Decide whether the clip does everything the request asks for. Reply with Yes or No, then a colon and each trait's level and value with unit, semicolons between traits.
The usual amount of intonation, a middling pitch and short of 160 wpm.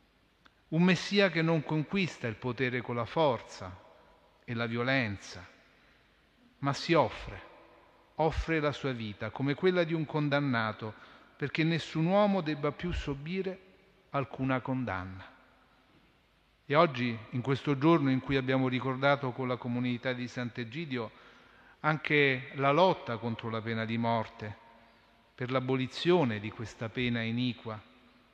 No: average, 4.7 semitones; low, 130 Hz; average, 130 wpm